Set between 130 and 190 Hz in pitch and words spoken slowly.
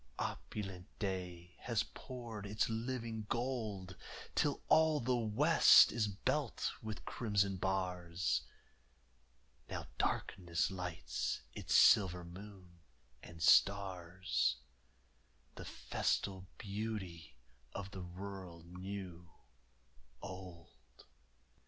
No: very low, 95 Hz; slow, 90 wpm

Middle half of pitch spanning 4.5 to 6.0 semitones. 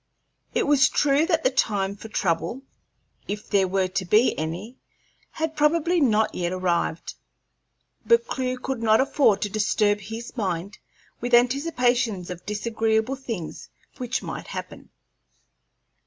Yes: average, 5.3 semitones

